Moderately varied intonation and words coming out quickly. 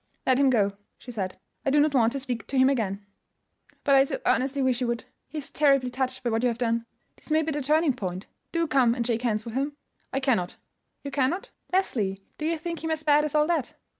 Yes: average, 4.1 semitones; fast, 245 wpm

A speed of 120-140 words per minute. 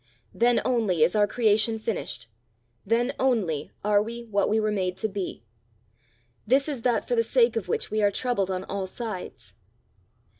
No: average, 175 wpm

